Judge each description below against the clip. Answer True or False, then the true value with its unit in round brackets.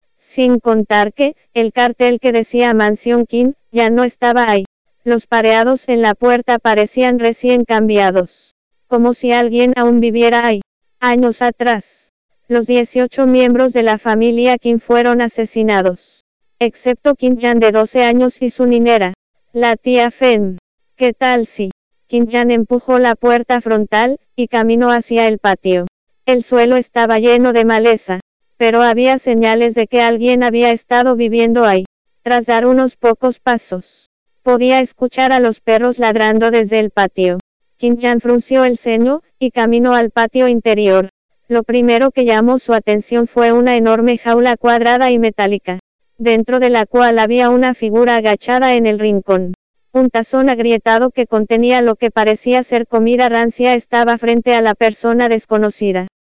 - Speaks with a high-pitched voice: True (235 Hz)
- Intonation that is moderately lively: False (1.6 semitones)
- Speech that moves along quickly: False (155 wpm)